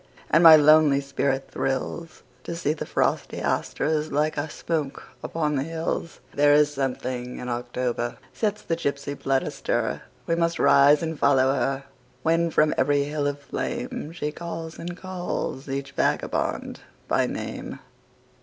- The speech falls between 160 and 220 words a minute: No, slow, 135 wpm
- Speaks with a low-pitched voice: No, medium, 145 Hz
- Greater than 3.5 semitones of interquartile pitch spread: No, average, 3.2 semitones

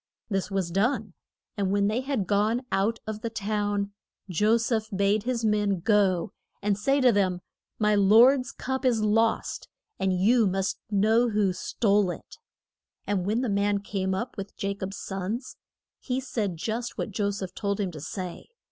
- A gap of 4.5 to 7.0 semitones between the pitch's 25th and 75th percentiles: No, narrow, 2.6 semitones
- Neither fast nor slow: Yes, average, 175 wpm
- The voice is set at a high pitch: Yes, high, 205 Hz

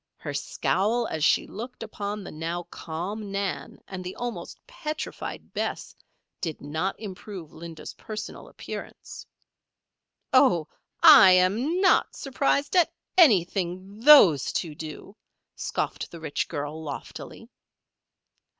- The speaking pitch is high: Yes, high, 195 Hz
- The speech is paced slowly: Yes, slow, 115 wpm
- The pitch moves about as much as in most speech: No, wide, 5.8 semitones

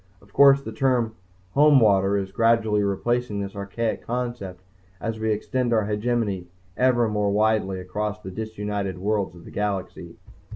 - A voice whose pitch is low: Yes, low, 105 Hz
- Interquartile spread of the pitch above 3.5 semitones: No, average, 2.8 semitones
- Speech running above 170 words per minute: No, average, 150 wpm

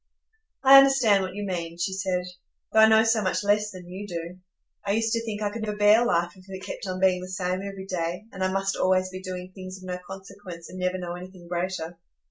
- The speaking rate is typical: No, fast, 240 wpm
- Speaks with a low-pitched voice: No, medium, 185 Hz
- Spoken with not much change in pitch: Yes, narrow, 2.2 semitones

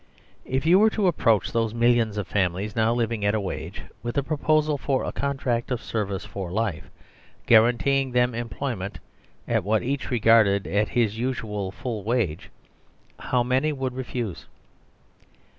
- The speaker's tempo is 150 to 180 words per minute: Yes, average, 155 wpm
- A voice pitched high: No, low, 115 Hz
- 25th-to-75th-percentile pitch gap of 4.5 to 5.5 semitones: No, average, 4.0 semitones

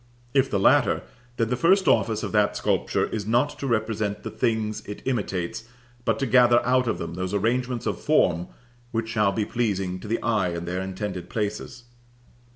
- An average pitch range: Yes, average, 3.6 semitones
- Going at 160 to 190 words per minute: Yes, average, 185 wpm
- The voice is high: No, low, 110 Hz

